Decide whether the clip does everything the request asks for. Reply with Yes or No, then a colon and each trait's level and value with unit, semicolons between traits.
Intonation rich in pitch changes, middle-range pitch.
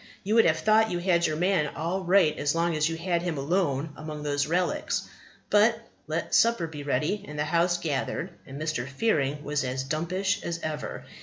No: average, 3.5 semitones; medium, 165 Hz